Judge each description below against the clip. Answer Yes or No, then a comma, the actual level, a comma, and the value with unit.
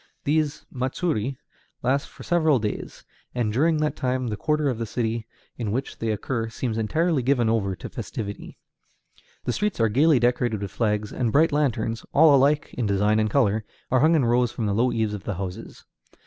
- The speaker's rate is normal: Yes, average, 190 wpm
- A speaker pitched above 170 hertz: No, low, 120 Hz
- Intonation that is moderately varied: Yes, average, 4.5 semitones